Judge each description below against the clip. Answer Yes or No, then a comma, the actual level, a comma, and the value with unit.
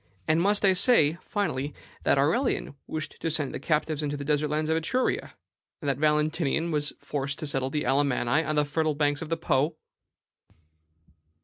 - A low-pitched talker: No, medium, 150 Hz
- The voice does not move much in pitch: Yes, narrow, 2.1 semitones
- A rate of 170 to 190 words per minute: Yes, average, 180 wpm